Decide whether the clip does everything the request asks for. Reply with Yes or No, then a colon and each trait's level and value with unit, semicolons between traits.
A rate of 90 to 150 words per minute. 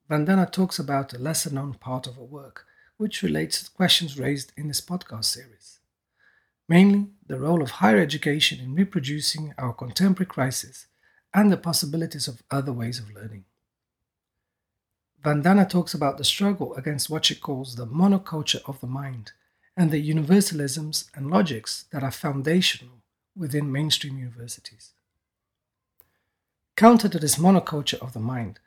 Yes: average, 145 wpm